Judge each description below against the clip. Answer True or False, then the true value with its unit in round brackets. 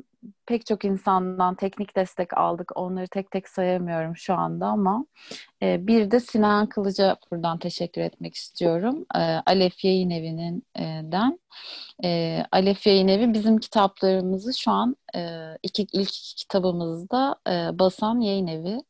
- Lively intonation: False (3.6 semitones)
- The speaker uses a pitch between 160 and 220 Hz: True (190 Hz)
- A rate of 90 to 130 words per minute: False (140 wpm)